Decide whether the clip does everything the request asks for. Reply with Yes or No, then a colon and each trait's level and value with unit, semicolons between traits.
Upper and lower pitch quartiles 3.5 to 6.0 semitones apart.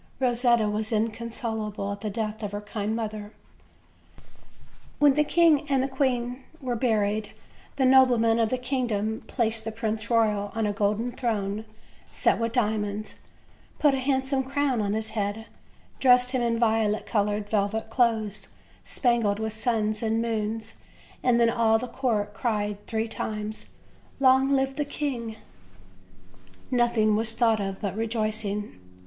No: average, 2.7 semitones